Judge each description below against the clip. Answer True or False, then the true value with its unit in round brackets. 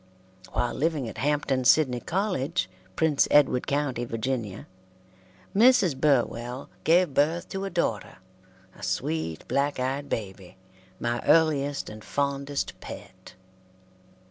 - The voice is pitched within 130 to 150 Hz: True (140 Hz)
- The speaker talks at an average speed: False (115 wpm)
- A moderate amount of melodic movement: True (4.2 semitones)